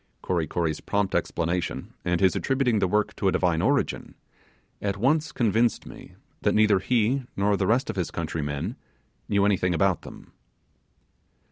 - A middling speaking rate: Yes, average, 160 wpm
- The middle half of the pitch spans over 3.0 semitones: Yes, average, 4.1 semitones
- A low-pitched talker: Yes, low, 100 Hz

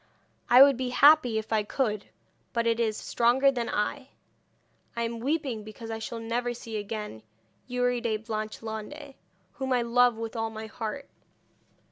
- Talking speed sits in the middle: Yes, average, 160 wpm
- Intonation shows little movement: Yes, narrow, 2.2 semitones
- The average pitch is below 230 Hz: No, high, 235 Hz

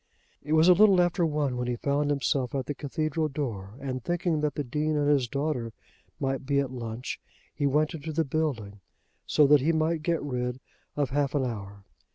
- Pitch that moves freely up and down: No, average, 3.4 semitones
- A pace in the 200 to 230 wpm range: Yes, fast, 205 wpm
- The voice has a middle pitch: Yes, medium, 145 Hz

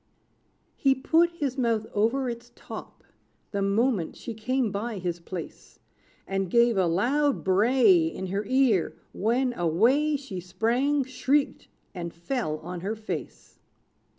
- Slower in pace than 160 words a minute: Yes, slow, 135 wpm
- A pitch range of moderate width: No, wide, 5.7 semitones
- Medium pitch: No, high, 225 Hz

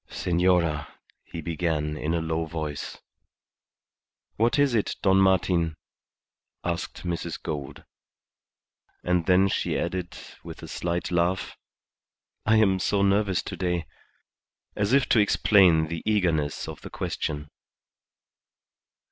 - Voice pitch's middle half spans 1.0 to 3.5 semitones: Yes, average, 3.1 semitones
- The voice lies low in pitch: Yes, very low, 85 Hz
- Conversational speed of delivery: No, slow, 120 wpm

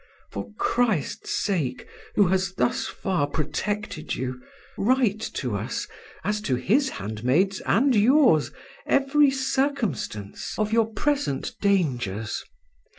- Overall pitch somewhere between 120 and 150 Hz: No, high, 195 Hz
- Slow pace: Yes, slow, 110 wpm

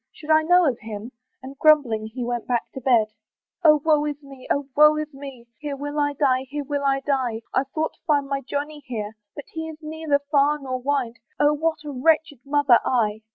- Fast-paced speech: Yes, fast, 215 wpm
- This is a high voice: Yes, very high, 280 Hz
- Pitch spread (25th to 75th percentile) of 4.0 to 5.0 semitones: No, average, 2.8 semitones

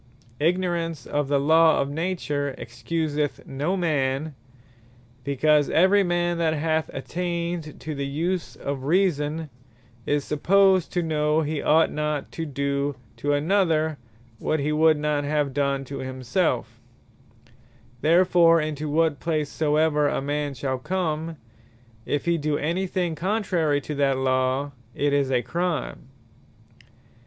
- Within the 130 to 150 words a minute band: Yes, slow, 135 wpm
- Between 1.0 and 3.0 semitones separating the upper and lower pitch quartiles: Yes, average, 2.7 semitones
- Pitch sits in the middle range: Yes, medium, 150 Hz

